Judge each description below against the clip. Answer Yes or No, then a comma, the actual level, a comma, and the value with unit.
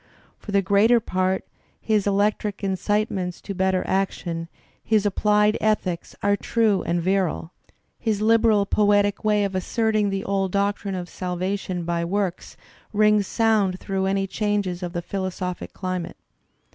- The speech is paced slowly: No, average, 150 wpm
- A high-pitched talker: Yes, high, 200 Hz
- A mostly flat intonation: Yes, narrow, 2.1 semitones